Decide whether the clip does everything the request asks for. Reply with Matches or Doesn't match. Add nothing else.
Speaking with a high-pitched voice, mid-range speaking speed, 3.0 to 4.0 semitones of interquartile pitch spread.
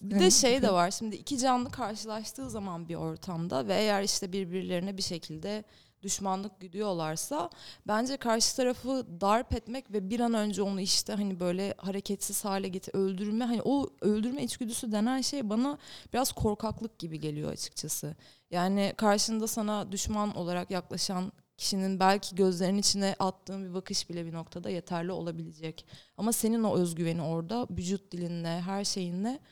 Doesn't match